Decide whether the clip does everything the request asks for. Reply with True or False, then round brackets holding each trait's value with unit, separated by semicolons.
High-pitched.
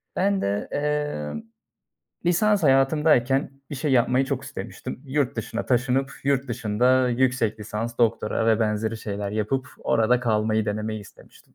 False (125 Hz)